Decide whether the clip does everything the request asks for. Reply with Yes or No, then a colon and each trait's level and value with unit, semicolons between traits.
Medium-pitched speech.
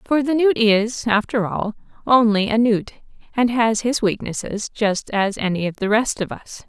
No: high, 220 Hz